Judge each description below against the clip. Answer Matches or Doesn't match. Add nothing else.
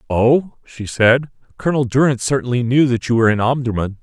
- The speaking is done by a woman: Doesn't match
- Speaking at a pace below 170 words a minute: Doesn't match